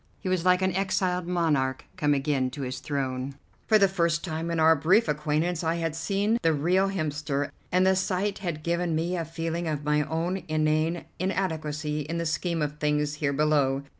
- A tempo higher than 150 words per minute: Yes, average, 195 wpm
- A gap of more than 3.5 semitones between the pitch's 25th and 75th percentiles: No, average, 3.2 semitones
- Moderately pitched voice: Yes, medium, 160 Hz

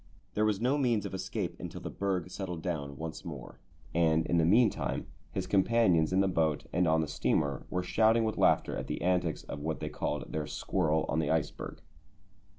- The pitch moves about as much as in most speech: Yes, average, 3.7 semitones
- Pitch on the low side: Yes, very low, 90 Hz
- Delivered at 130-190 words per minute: No, average, 200 wpm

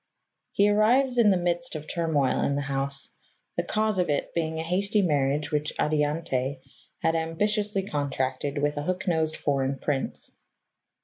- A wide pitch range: No, average, 4.8 semitones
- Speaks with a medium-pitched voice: Yes, medium, 160 Hz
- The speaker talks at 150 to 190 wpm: Yes, average, 160 wpm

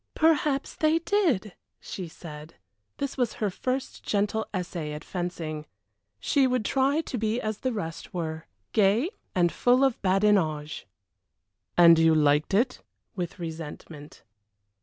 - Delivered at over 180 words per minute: No, slow, 135 wpm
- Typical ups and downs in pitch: No, wide, 7.6 semitones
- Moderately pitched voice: No, high, 195 Hz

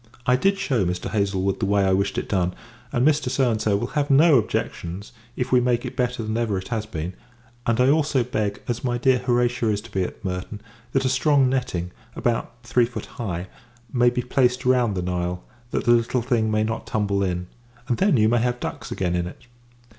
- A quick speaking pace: Yes, fast, 215 wpm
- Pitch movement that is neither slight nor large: Yes, average, 4.1 semitones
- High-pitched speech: No, low, 115 Hz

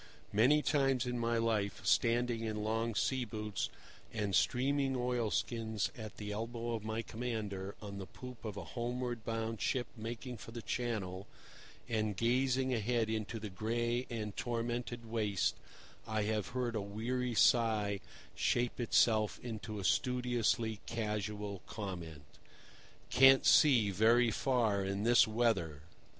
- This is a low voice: Yes, low, 115 Hz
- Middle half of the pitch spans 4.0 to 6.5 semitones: No, narrow, 2.4 semitones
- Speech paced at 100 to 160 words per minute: Yes, slow, 135 wpm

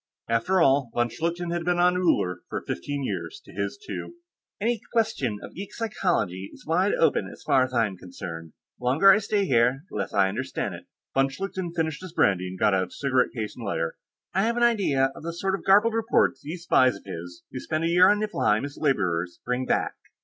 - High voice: No, medium, 140 Hz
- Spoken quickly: Yes, fast, 215 wpm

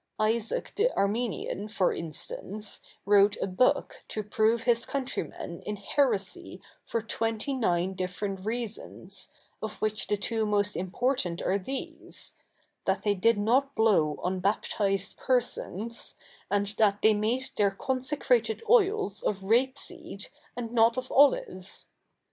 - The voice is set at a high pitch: Yes, high, 215 Hz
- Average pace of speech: No, slow, 130 wpm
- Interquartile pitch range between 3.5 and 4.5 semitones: Yes, average, 3.8 semitones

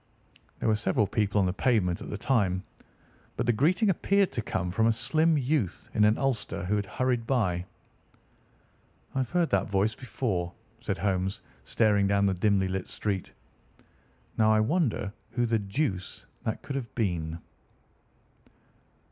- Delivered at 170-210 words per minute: No, average, 155 wpm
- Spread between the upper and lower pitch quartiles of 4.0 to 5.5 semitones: Yes, average, 4.8 semitones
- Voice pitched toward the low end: Yes, low, 105 Hz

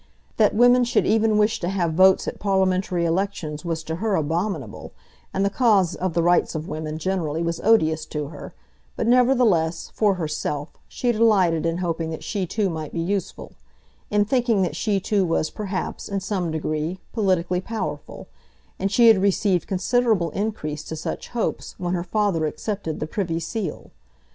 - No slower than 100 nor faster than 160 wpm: No, average, 175 wpm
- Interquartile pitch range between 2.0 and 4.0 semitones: No, average, 4.4 semitones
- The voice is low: No, medium, 185 Hz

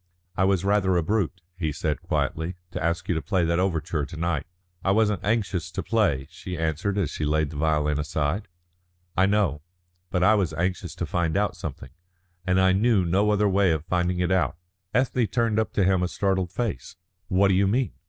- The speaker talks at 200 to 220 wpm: Yes, fast, 205 wpm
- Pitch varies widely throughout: No, average, 3.6 semitones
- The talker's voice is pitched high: No, very low, 90 Hz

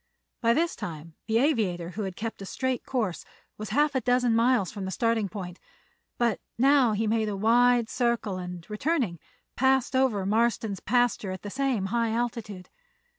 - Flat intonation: No, average, 4.0 semitones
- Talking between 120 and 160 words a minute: No, average, 175 wpm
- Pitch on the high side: Yes, high, 225 Hz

